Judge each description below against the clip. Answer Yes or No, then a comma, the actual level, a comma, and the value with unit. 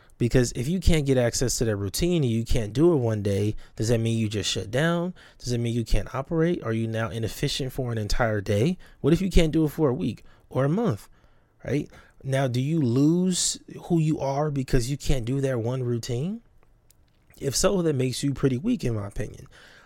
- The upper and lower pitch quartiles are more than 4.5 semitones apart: Yes, average, 5.2 semitones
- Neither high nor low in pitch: No, low, 130 Hz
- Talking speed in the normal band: No, fast, 225 wpm